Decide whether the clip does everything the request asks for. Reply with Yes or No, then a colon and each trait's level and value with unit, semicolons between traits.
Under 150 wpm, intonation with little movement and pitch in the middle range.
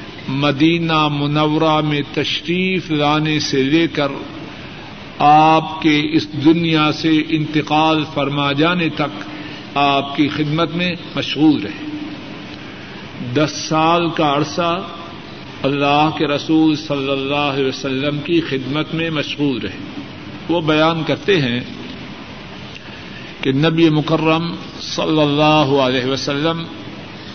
Yes: slow, 110 wpm; narrow, 1.9 semitones; medium, 150 Hz